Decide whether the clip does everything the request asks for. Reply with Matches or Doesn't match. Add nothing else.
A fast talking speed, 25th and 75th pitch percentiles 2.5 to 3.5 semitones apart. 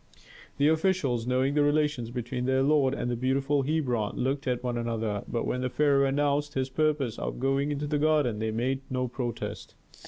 Doesn't match